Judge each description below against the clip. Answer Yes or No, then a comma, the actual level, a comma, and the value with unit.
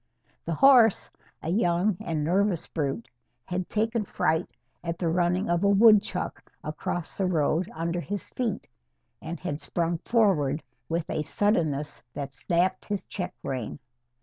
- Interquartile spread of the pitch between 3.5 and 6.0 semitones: Yes, average, 3.9 semitones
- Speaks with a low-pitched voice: No, medium, 175 Hz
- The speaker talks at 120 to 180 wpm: Yes, average, 145 wpm